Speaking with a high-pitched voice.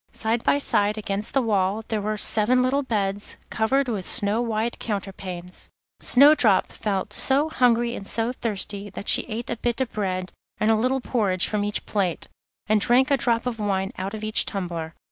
Yes: high, 215 Hz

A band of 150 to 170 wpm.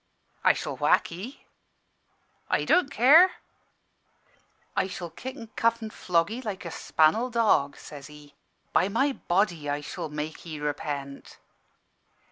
No: average, 140 wpm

